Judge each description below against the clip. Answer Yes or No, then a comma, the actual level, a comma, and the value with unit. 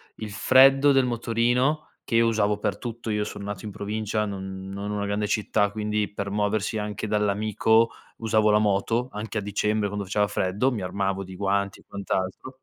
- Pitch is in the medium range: No, low, 105 Hz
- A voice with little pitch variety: Yes, narrow, 1.9 semitones